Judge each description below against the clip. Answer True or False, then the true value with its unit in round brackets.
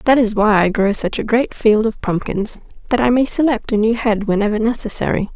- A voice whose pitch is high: True (220 Hz)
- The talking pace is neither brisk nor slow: False (215 wpm)